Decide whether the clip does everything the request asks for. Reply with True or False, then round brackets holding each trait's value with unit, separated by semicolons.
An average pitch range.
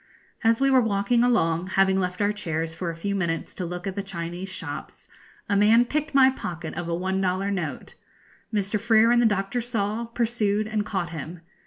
True (4.1 semitones)